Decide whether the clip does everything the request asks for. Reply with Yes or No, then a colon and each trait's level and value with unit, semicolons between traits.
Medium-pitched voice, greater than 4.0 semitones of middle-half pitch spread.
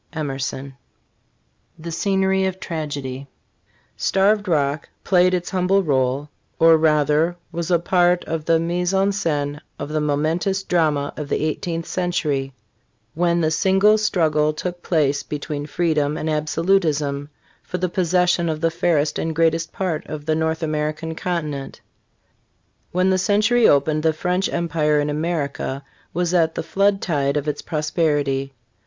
No: medium, 160 Hz; average, 3.1 semitones